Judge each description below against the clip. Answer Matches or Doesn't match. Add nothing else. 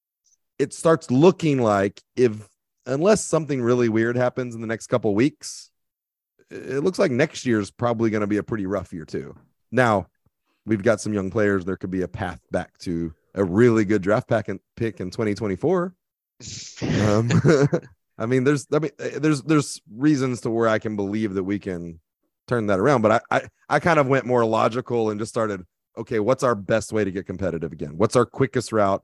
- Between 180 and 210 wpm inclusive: Matches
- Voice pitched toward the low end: Matches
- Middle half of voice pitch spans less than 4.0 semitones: Doesn't match